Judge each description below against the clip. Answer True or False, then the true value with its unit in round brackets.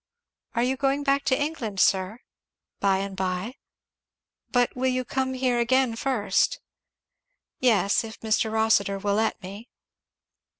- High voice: True (230 Hz)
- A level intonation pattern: False (4.5 semitones)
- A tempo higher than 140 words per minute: False (135 wpm)